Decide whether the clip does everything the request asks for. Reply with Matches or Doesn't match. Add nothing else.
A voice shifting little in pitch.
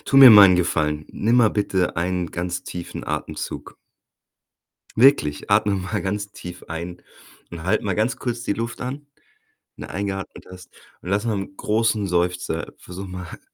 Doesn't match